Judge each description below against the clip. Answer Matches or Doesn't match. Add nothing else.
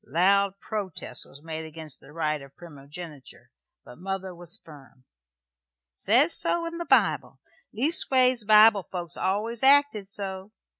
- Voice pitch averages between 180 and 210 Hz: Matches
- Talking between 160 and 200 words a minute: Doesn't match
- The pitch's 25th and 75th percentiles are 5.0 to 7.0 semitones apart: Matches